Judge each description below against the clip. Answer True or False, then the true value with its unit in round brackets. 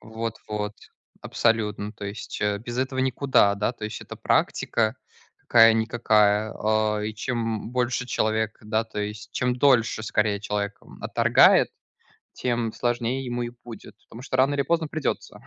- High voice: False (110 Hz)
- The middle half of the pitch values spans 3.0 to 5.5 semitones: False (2.4 semitones)